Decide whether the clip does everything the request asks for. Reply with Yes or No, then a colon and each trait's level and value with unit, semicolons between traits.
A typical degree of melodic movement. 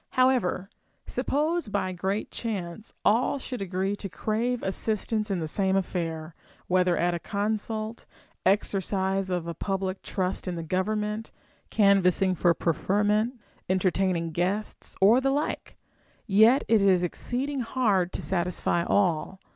Yes: average, 3.1 semitones